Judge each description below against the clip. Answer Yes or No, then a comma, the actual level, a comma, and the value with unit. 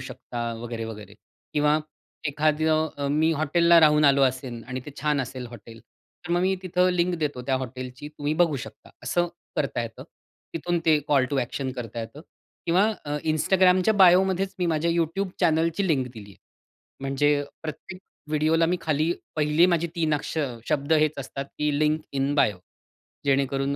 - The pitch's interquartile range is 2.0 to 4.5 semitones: Yes, average, 3.7 semitones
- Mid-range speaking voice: Yes, medium, 150 Hz